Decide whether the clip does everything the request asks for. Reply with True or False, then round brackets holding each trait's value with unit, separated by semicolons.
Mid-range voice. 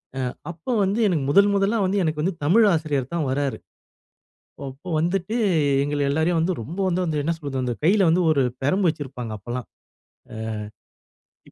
True (160 Hz)